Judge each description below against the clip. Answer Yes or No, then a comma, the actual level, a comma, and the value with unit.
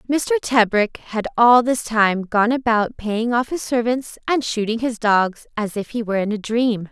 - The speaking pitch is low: No, high, 230 Hz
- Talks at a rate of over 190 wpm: Yes, average, 200 wpm